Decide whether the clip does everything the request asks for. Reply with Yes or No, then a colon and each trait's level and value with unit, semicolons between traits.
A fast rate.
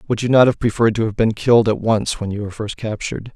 Yes: fast, 285 wpm